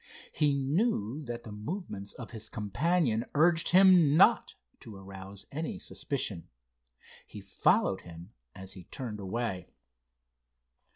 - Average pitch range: No, wide, 7.5 semitones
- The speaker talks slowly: Yes, slow, 120 wpm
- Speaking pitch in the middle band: No, low, 115 Hz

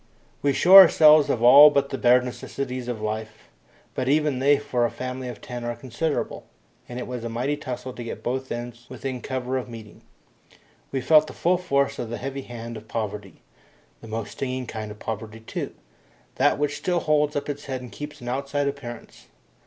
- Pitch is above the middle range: No, low, 125 Hz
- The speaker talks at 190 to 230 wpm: Yes, average, 200 wpm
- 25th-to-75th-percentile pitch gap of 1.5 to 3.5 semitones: Yes, average, 3.1 semitones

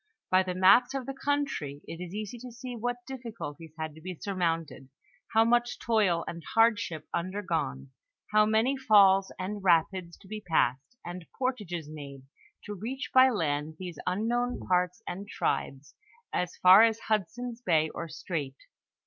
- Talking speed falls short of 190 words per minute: Yes, average, 160 wpm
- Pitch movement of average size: No, wide, 5.7 semitones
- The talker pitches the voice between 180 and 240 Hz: Yes, high, 190 Hz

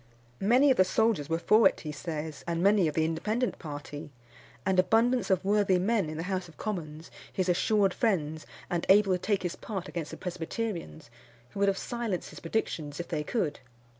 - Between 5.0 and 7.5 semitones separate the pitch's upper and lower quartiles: No, average, 4.6 semitones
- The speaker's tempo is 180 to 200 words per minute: Yes, average, 195 wpm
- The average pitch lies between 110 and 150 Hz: No, medium, 185 Hz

